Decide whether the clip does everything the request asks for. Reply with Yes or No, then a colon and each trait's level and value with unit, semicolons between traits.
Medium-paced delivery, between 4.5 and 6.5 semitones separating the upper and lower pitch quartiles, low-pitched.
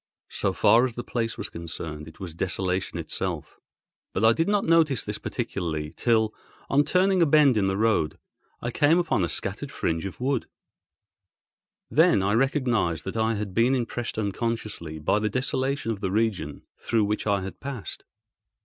Yes: average, 175 wpm; average, 5.3 semitones; low, 110 Hz